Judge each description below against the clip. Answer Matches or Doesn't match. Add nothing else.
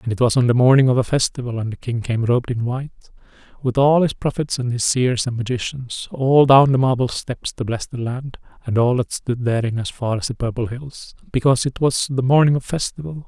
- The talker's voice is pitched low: Matches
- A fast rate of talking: Matches